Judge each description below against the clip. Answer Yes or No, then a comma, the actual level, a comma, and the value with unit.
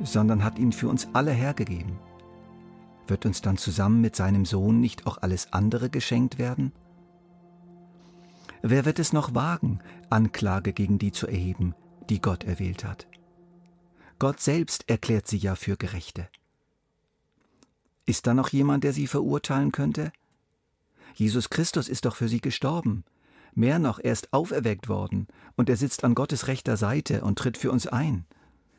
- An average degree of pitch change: No, wide, 6.1 semitones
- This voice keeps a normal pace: Yes, average, 155 wpm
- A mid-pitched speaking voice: No, low, 115 Hz